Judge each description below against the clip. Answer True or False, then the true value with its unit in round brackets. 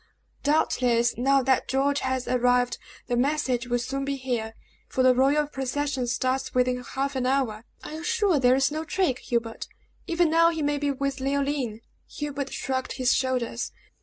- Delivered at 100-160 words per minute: False (170 wpm)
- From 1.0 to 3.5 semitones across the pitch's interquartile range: True (2.5 semitones)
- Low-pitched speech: False (265 Hz)